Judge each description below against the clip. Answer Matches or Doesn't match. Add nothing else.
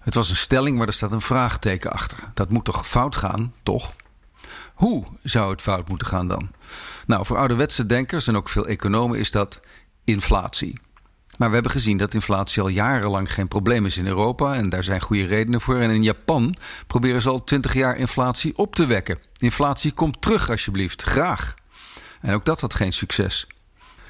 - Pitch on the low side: Matches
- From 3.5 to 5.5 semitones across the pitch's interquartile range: Matches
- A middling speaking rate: Matches